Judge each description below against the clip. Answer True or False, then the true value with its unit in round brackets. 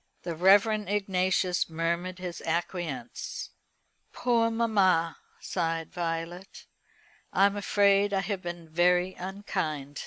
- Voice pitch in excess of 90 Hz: True (185 Hz)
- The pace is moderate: False (105 wpm)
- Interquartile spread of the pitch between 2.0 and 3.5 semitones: True (3.0 semitones)